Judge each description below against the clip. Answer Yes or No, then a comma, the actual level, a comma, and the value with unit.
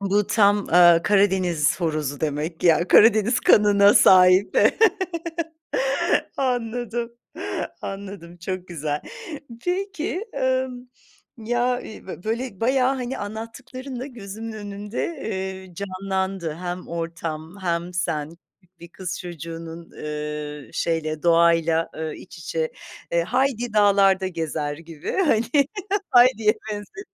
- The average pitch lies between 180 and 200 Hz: Yes, high, 190 Hz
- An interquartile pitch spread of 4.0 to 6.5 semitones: Yes, average, 5.3 semitones